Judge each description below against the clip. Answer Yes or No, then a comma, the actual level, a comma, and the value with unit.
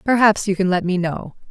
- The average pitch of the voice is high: Yes, high, 195 Hz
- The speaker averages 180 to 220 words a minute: No, fast, 240 wpm